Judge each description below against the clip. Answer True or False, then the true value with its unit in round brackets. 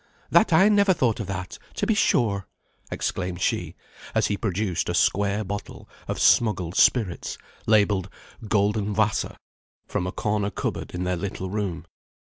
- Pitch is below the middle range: True (100 Hz)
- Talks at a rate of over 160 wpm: False (150 wpm)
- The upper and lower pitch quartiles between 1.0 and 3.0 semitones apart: True (2.7 semitones)